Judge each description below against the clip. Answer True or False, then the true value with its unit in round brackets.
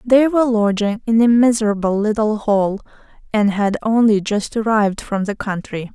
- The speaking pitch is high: True (215 Hz)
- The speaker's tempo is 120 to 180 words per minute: True (160 wpm)